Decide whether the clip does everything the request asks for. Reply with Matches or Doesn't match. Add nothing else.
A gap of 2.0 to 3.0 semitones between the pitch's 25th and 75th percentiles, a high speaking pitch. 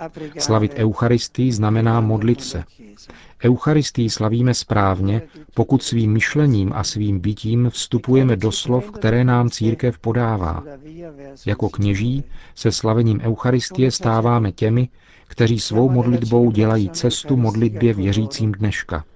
Doesn't match